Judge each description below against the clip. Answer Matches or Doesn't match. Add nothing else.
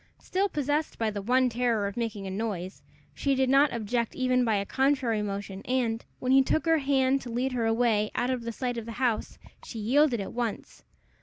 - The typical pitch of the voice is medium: Doesn't match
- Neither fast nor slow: Doesn't match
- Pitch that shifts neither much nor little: Matches